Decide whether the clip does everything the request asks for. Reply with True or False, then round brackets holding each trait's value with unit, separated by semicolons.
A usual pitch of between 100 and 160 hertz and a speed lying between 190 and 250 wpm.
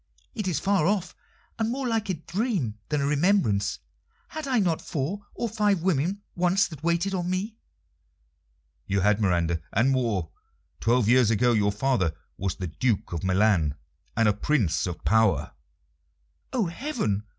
False (140 Hz; 160 wpm)